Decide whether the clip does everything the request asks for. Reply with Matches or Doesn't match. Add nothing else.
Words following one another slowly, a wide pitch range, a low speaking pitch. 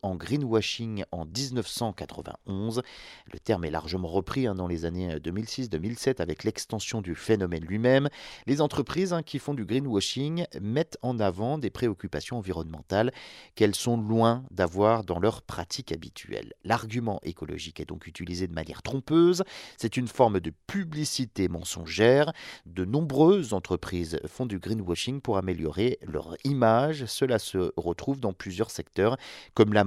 Matches